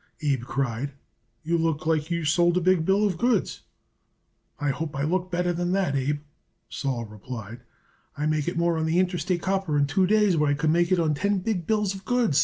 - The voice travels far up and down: No, average, 4.1 semitones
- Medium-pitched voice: Yes, medium, 165 Hz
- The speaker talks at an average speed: No, fast, 210 wpm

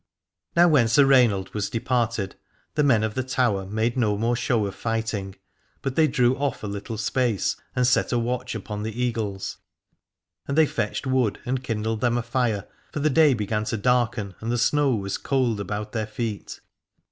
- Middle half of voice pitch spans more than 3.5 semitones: No, average, 3.1 semitones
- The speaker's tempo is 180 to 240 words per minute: Yes, average, 190 wpm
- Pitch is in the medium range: No, low, 115 Hz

